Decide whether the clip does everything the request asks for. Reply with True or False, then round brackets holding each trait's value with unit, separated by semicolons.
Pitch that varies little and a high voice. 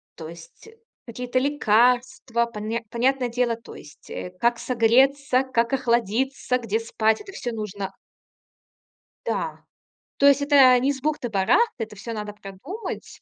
False (3.3 semitones; 240 Hz)